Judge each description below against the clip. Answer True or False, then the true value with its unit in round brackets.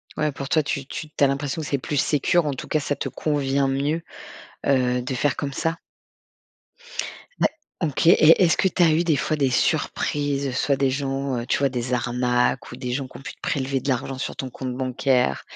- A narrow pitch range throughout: True (2.3 semitones)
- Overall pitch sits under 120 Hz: False (140 Hz)